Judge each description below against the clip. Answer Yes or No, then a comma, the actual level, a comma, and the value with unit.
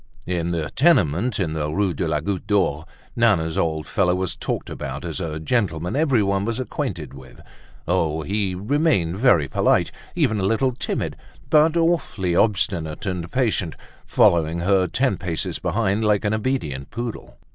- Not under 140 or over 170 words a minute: Yes, average, 155 wpm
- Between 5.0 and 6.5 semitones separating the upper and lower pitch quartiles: Yes, wide, 5.6 semitones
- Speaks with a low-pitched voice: Yes, very low, 95 Hz